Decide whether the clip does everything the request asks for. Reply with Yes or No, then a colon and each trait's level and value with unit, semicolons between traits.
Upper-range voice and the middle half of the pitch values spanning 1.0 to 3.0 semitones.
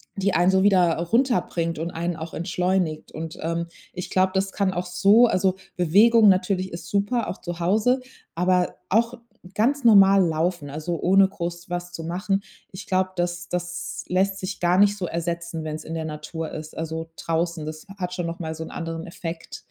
No: medium, 175 Hz; narrow, 2.6 semitones